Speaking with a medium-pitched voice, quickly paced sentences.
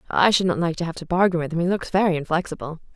Yes: medium, 170 Hz; fast, 285 wpm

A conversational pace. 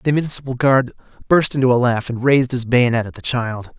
No: fast, 220 wpm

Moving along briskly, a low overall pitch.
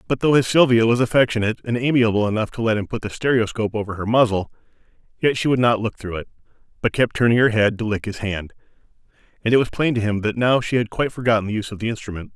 Yes: fast, 250 wpm; low, 115 Hz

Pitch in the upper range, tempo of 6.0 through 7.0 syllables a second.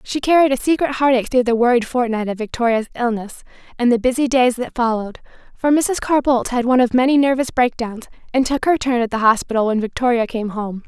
Yes: high, 245 Hz; 6.1 syllables/s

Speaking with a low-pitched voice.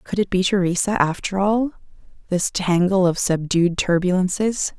No: medium, 185 Hz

